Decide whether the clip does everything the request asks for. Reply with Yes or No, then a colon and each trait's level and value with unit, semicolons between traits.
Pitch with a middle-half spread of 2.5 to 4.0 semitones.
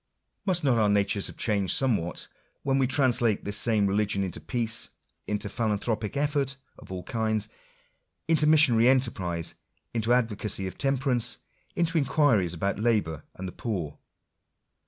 No: average, 4.9 semitones